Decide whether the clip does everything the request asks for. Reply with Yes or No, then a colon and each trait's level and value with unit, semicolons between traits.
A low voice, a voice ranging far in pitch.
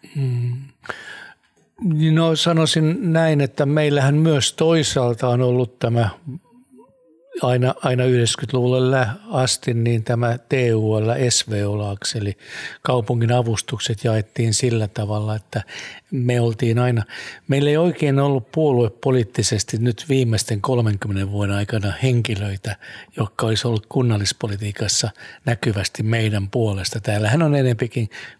No: low, 120 Hz; average, 3.7 semitones